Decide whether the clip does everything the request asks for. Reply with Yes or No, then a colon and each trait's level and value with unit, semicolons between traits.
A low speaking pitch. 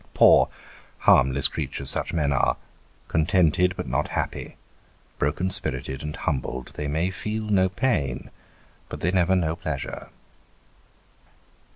Yes: very low, 80 Hz